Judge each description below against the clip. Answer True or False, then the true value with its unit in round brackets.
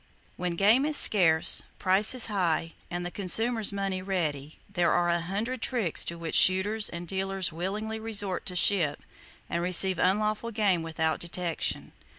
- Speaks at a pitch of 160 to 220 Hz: True (185 Hz)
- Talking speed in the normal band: True (155 wpm)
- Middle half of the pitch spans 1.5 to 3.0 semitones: False (3.5 semitones)